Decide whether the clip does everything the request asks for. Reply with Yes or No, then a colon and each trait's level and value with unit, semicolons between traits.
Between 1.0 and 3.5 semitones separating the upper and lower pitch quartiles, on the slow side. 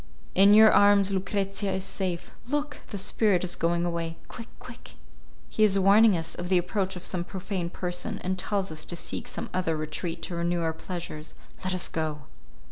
No: narrow, 2.6 semitones; average, 190 wpm